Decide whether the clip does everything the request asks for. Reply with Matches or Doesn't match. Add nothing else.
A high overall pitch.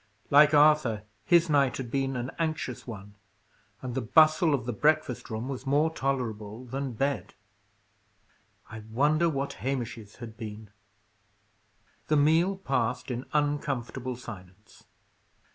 Doesn't match